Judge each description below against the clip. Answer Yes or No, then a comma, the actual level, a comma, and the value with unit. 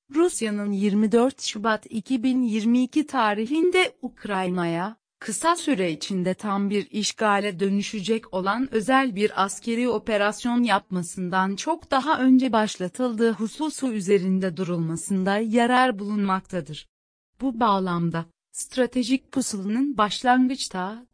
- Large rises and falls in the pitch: No, average, 4.6 semitones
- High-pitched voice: Yes, high, 220 Hz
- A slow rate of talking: Yes, slow, 95 wpm